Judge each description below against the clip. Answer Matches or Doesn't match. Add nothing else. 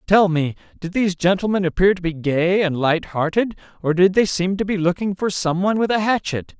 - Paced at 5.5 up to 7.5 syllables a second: Matches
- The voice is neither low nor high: Matches